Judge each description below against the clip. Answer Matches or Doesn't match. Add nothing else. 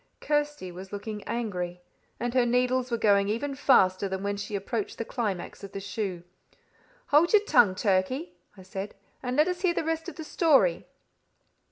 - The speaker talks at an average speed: Matches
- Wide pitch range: Matches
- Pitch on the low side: Doesn't match